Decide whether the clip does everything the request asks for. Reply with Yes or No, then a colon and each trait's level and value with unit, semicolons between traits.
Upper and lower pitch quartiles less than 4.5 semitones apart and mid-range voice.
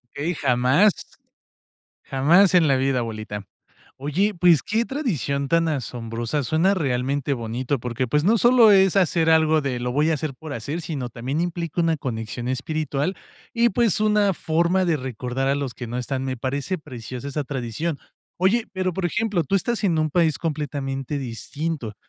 No: average, 5.2 semitones; medium, 150 Hz